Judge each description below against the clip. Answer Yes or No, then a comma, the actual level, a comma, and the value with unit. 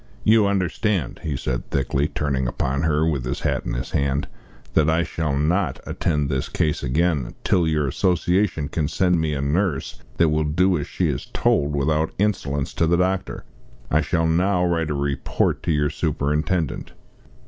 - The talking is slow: No, average, 175 wpm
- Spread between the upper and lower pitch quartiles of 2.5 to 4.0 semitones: Yes, average, 3.7 semitones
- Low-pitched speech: Yes, very low, 80 Hz